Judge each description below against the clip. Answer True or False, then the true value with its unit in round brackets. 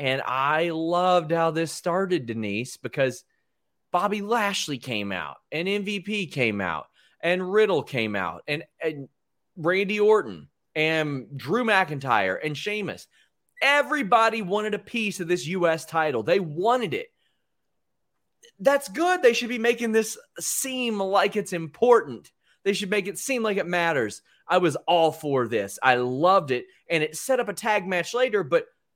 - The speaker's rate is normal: True (160 wpm)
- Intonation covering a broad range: True (6.0 semitones)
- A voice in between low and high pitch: True (180 Hz)